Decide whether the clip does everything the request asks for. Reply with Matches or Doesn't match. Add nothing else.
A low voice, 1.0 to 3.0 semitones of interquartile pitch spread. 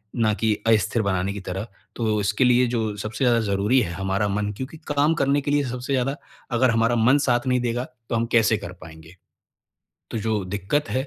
Doesn't match